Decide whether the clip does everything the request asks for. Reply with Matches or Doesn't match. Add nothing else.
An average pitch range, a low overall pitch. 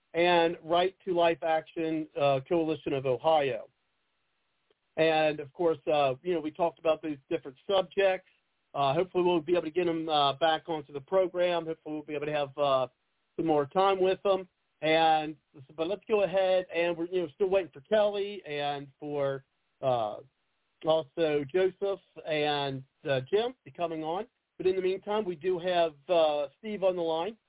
Doesn't match